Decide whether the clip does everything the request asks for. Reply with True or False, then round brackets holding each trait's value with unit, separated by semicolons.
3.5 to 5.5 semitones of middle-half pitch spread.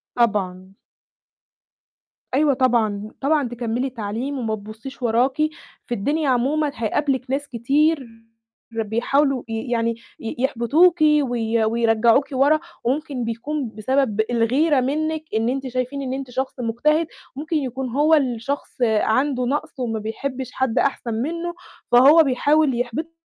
True (3.8 semitones)